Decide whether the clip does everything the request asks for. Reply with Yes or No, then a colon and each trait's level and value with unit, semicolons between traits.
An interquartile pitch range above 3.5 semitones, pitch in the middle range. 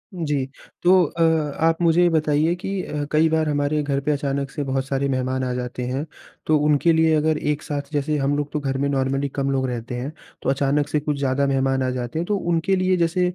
No: average, 2.8 semitones; medium, 145 Hz